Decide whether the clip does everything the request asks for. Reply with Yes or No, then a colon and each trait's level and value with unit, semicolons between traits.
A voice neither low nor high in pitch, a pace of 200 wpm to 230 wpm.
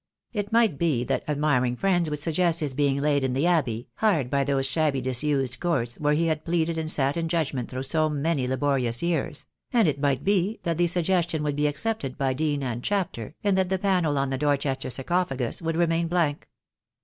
Yes: medium, 150 Hz; fast, 205 wpm